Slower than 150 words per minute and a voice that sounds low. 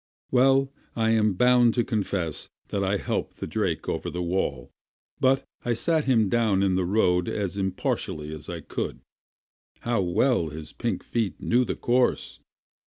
No: average, 165 wpm; low, 105 Hz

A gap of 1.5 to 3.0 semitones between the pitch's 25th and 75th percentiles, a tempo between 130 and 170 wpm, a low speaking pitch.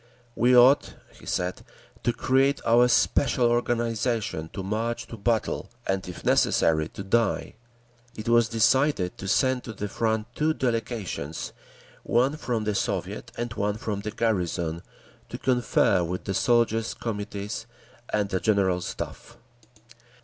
No: average, 3.5 semitones; average, 140 wpm; low, 110 Hz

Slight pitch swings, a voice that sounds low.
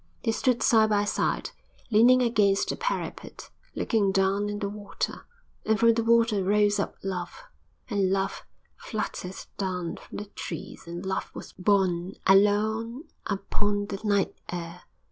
No: narrow, 2.2 semitones; high, 205 Hz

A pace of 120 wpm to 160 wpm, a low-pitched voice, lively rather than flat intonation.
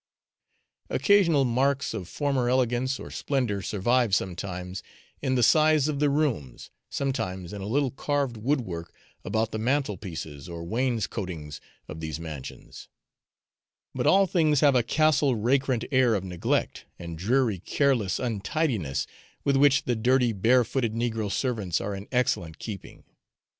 Yes: average, 140 wpm; low, 120 Hz; wide, 6.1 semitones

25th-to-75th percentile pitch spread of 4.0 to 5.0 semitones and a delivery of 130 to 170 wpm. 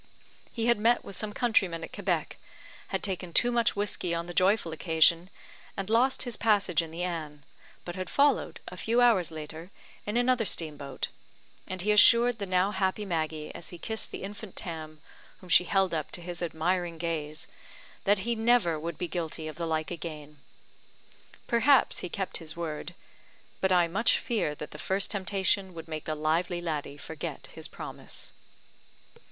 No: average, 4.3 semitones; average, 180 wpm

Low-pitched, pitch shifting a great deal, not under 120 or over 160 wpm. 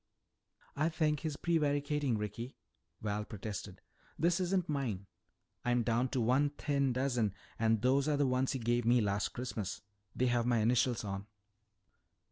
No: low, 125 Hz; average, 4.3 semitones; average, 150 wpm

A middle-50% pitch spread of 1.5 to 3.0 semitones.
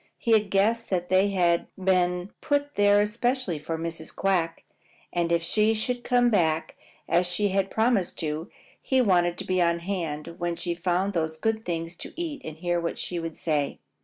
No: average, 3.7 semitones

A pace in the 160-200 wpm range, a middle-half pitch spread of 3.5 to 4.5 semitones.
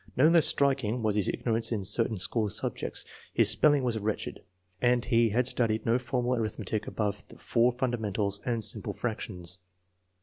No: average, 165 wpm; average, 2.7 semitones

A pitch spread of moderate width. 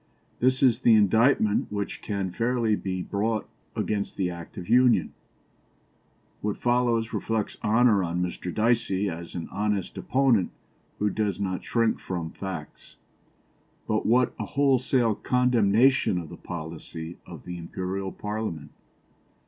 Yes: average, 4.2 semitones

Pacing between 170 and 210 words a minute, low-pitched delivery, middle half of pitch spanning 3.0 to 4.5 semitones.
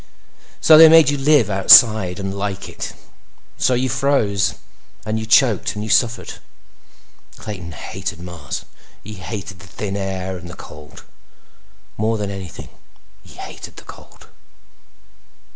No: average, 140 wpm; low, 100 Hz; average, 3.4 semitones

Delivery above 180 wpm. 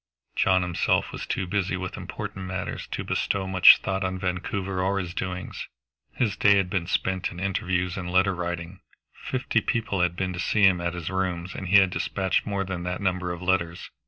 Yes: average, 200 wpm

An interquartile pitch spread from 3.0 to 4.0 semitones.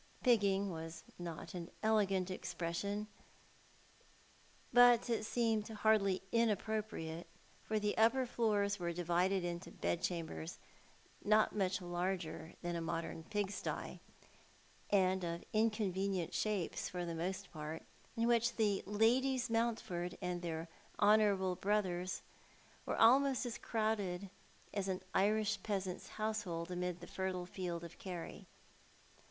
Yes: average, 3.6 semitones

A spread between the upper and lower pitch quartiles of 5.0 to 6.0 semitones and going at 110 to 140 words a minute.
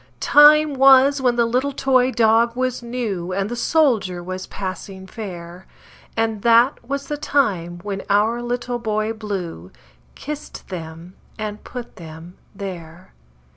Yes: average, 5.3 semitones; slow, 135 wpm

